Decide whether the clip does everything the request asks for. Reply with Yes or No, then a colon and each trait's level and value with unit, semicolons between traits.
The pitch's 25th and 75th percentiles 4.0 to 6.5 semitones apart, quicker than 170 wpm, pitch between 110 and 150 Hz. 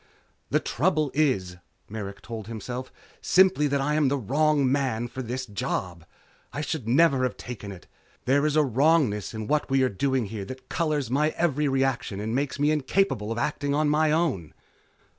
Yes: average, 4.9 semitones; average, 180 wpm; low, 135 Hz